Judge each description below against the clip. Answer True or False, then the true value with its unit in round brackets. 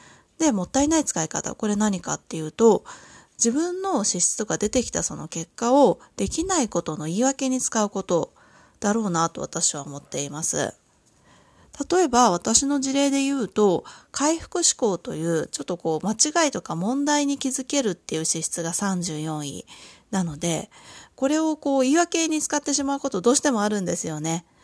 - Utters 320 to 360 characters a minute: True (340 characters per minute)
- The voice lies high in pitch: True (225 Hz)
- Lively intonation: True (8.5 semitones)